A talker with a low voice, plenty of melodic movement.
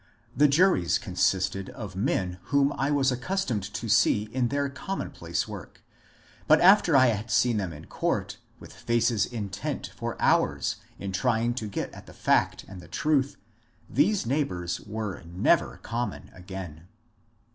Yes: low, 115 Hz; wide, 6.4 semitones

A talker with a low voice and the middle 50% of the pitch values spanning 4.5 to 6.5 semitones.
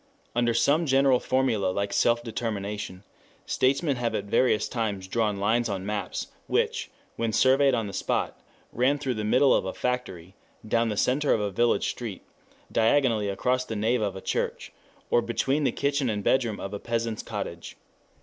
No: low, 115 Hz; average, 3.8 semitones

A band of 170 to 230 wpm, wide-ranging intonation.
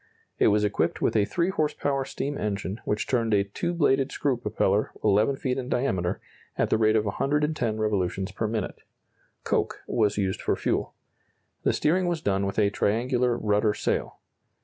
No: average, 175 wpm; average, 4.8 semitones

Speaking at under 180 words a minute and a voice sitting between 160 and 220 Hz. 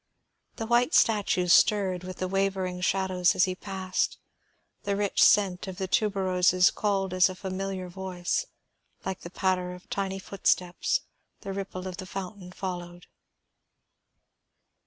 Yes: slow, 135 wpm; high, 190 Hz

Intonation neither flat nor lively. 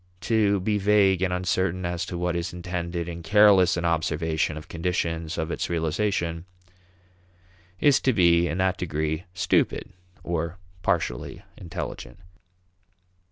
No: narrow, 2.2 semitones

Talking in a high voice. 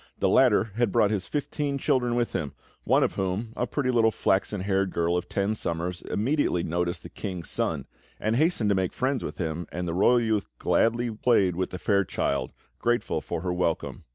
No: low, 100 Hz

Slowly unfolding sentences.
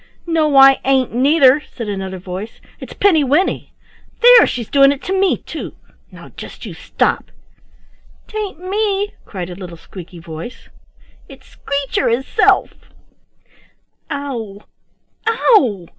Yes: slow, 125 wpm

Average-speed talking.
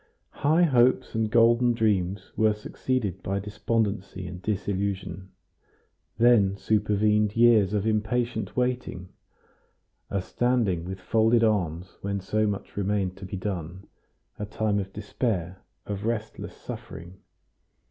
No: slow, 120 wpm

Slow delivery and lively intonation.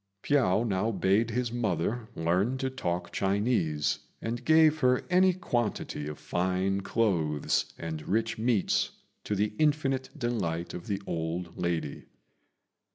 Yes: slow, 130 wpm; wide, 5.9 semitones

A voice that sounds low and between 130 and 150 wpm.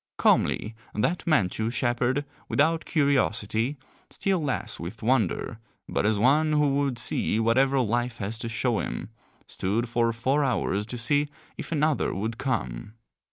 Yes: low, 120 Hz; average, 145 wpm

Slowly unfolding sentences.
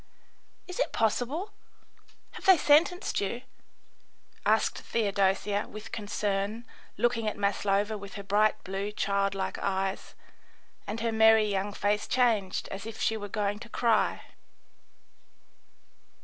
Yes: slow, 125 wpm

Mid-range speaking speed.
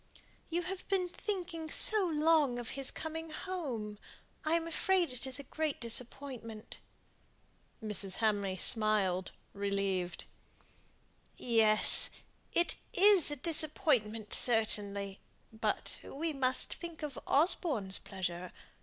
No: slow, 110 wpm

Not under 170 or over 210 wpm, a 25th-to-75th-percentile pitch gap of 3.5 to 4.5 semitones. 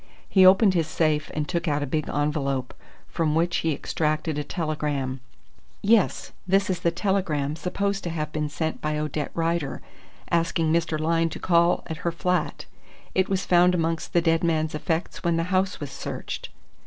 No: average, 180 wpm; average, 2.7 semitones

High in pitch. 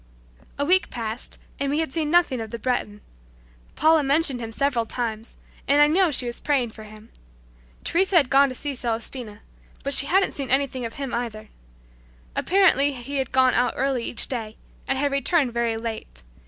Yes: very high, 260 Hz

